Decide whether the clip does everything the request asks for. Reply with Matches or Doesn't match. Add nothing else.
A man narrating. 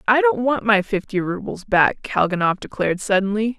Doesn't match